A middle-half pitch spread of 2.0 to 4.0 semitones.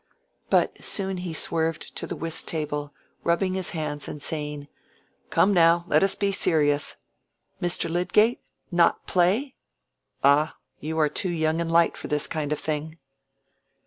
Yes: average, 2.8 semitones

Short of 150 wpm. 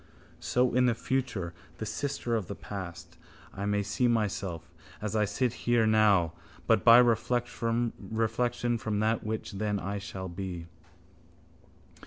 Yes: average, 140 wpm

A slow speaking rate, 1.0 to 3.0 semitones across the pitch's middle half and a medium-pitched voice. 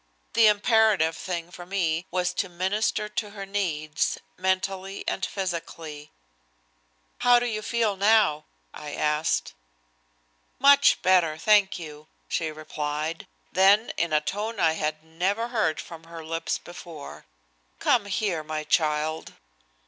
No: slow, 130 wpm; average, 4.5 semitones; medium, 175 Hz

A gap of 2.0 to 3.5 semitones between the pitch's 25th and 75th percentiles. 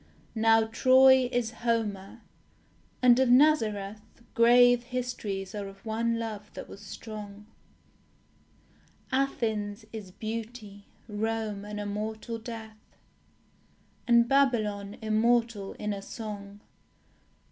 Yes: narrow, 2.5 semitones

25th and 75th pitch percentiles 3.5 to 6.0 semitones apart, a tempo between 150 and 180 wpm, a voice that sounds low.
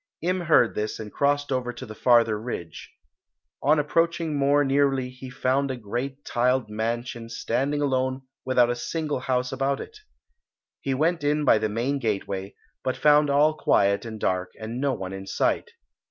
Yes: average, 3.9 semitones; average, 170 wpm; low, 130 Hz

